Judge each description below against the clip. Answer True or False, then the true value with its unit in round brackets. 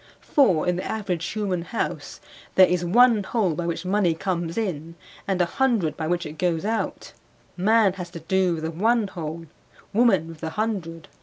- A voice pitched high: False (180 Hz)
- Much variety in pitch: False (4.1 semitones)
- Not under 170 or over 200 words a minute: True (185 wpm)